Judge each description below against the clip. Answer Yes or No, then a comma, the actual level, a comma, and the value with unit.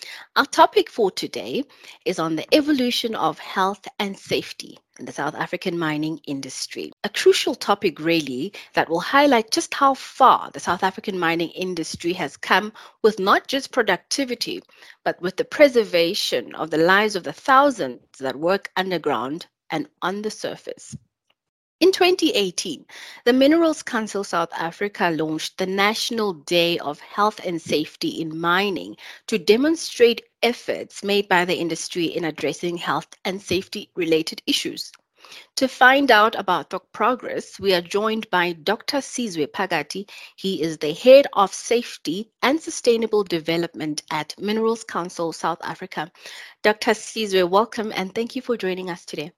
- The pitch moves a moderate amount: No, wide, 6.3 semitones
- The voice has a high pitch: Yes, high, 200 Hz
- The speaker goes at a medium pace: Yes, average, 150 wpm